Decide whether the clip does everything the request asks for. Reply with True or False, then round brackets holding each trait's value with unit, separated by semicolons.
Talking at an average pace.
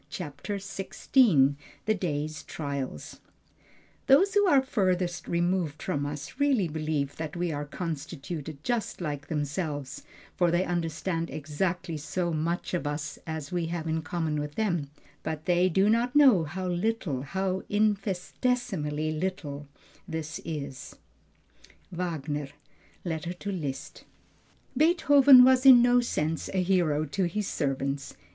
False (130 wpm)